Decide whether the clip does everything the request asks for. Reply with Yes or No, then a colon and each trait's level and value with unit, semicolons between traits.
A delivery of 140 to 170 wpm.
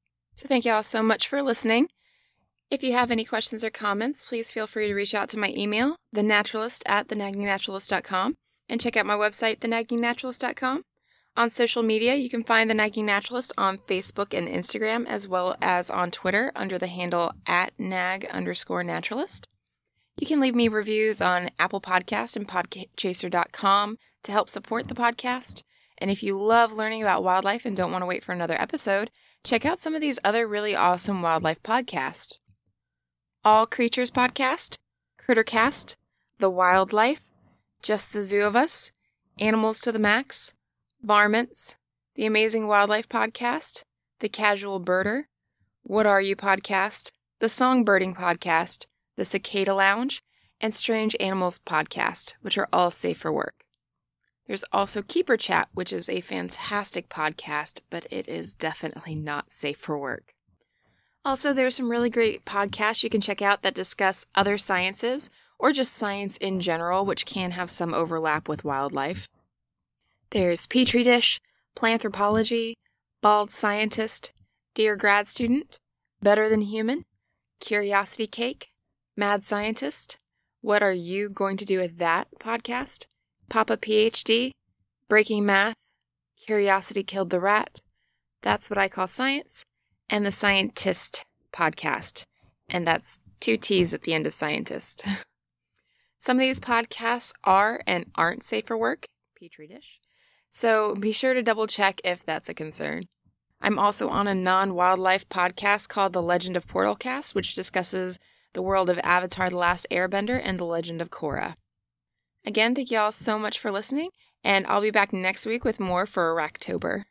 Yes: average, 155 wpm